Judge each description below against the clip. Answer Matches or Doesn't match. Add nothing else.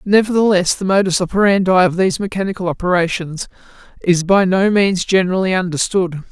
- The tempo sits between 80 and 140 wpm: Matches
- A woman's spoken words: Matches